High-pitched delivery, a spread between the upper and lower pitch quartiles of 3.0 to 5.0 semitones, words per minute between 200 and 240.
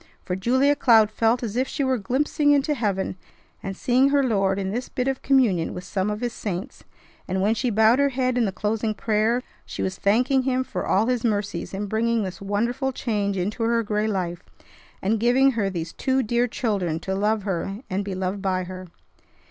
Yes: high, 220 Hz; average, 4.2 semitones; fast, 205 wpm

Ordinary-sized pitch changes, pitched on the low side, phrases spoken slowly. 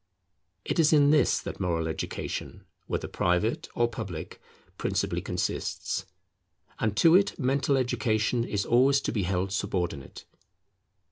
No: wide, 6.8 semitones; low, 115 Hz; slow, 130 wpm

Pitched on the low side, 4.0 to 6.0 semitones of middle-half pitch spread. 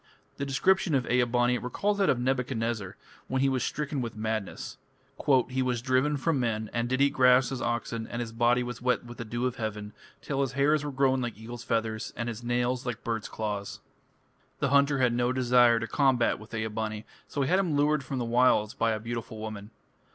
No: low, 120 Hz; narrow, 2.6 semitones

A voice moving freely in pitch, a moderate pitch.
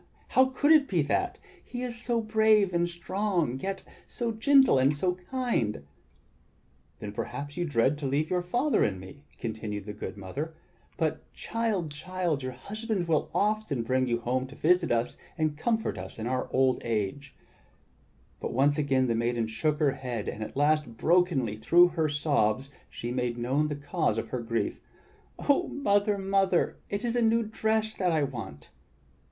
Yes: wide, 8.4 semitones; medium, 150 Hz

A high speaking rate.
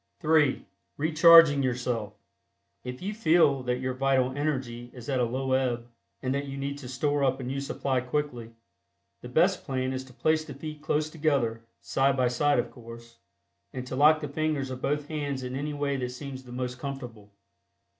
No: average, 190 wpm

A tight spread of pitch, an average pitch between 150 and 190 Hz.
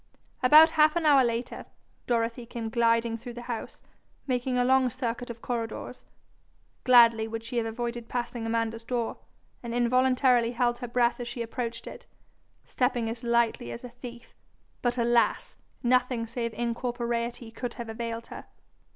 No: narrow, 1.3 semitones; high, 240 Hz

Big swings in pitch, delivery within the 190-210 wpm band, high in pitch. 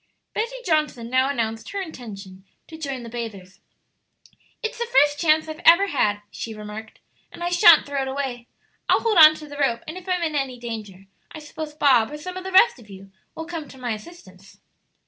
Yes: wide, 6.2 semitones; fast, 205 wpm; very high, 280 Hz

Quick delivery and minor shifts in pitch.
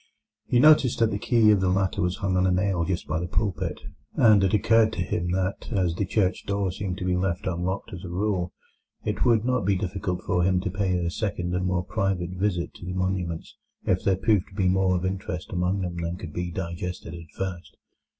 Yes: fast, 230 wpm; narrow, 2.1 semitones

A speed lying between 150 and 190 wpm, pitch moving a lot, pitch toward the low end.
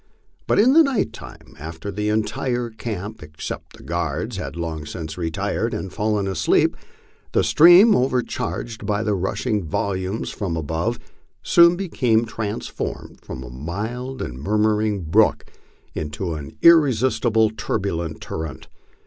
No: slow, 135 wpm; wide, 6.3 semitones; low, 105 Hz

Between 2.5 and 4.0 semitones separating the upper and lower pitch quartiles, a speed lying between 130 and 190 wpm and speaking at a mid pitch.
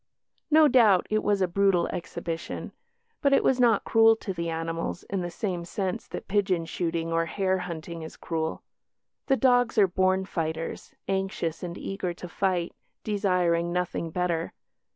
Yes: average, 3.1 semitones; average, 160 wpm; medium, 180 Hz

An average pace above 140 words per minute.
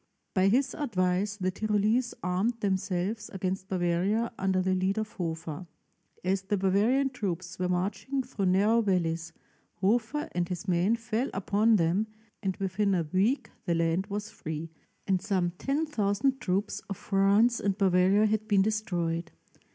Yes: average, 150 wpm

